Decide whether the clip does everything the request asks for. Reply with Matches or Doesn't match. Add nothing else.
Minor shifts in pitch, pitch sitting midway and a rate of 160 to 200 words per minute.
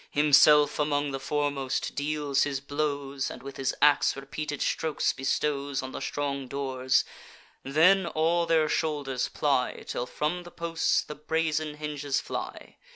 Doesn't match